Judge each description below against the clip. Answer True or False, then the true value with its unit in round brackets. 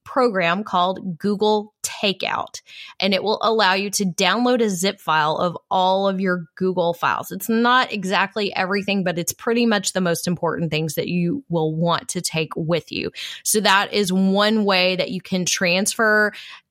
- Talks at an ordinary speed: True (175 wpm)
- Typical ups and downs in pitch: True (3.0 semitones)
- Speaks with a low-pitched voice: False (190 Hz)